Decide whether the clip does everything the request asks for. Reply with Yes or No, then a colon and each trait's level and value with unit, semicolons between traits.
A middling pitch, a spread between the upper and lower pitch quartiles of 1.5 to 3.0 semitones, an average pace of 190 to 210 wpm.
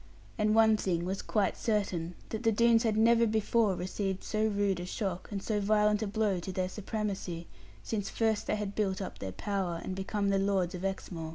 No: high, 200 Hz; narrow, 2.4 semitones; fast, 205 wpm